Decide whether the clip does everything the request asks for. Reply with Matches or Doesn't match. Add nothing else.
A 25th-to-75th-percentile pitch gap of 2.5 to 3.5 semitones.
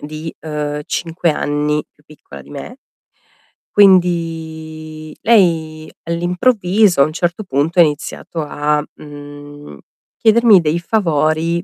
Matches